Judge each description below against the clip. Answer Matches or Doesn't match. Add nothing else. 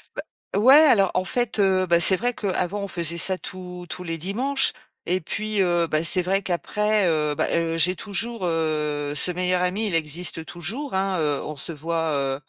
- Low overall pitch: Doesn't match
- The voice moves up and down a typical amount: Matches